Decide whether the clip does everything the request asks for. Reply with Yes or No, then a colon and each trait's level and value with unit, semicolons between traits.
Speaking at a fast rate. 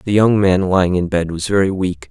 Yes: fast, 255 wpm